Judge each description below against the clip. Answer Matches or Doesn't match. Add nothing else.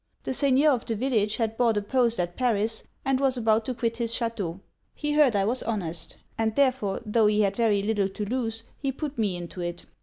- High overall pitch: Matches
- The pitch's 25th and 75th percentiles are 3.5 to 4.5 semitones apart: Matches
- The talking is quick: Matches